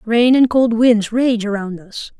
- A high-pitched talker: Yes, high, 225 Hz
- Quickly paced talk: No, average, 190 wpm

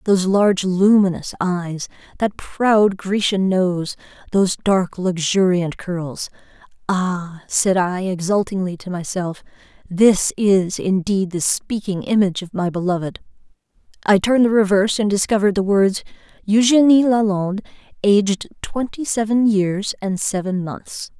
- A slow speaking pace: Yes, slow, 110 wpm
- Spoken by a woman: Yes, female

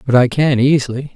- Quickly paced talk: Yes, fast, 210 wpm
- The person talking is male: Yes, male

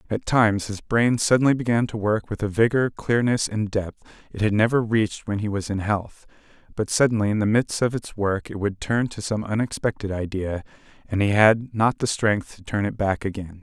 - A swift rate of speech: Yes, fast, 215 wpm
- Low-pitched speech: Yes, low, 105 Hz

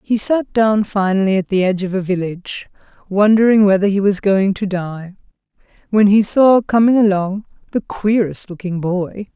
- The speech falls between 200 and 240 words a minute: No, average, 165 wpm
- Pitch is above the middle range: Yes, high, 200 Hz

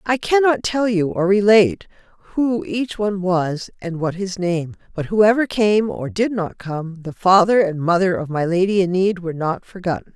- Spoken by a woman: Yes, female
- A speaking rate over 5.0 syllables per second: No, 4.9 syllables/s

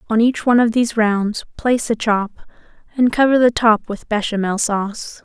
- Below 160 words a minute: No, average, 185 wpm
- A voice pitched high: Yes, high, 225 Hz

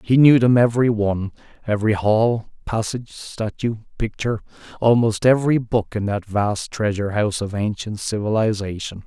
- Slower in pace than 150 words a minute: Yes, average, 140 wpm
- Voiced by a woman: No, male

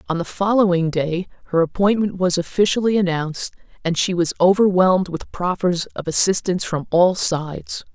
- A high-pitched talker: No, medium, 180 Hz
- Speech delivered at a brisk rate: No, average, 150 wpm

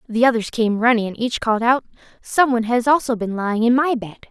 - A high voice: Yes, high, 235 Hz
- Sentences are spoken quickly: Yes, fast, 235 wpm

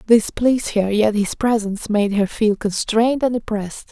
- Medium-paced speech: Yes, average, 185 wpm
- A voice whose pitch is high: Yes, high, 215 Hz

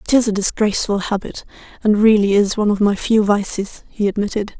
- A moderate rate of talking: Yes, average, 195 wpm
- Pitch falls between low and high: No, high, 205 Hz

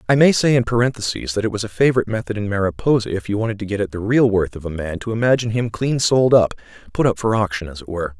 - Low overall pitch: Yes, low, 110 Hz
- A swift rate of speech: Yes, fast, 280 wpm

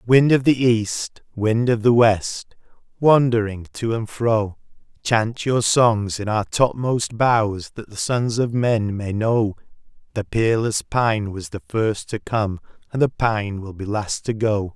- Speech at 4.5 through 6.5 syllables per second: No, 3.7 syllables/s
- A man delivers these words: Yes, male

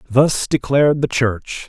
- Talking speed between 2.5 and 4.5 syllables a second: Yes, 4.0 syllables/s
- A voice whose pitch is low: Yes, low, 130 Hz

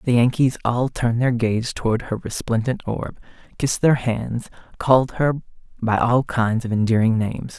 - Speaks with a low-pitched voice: Yes, low, 120 Hz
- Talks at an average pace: Yes, average, 165 wpm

